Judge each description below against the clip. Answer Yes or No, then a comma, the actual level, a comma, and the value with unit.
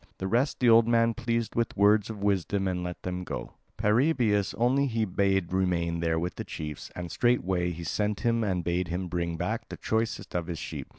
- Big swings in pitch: No, average, 4.5 semitones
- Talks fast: Yes, fast, 210 wpm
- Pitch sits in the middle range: No, very low, 95 Hz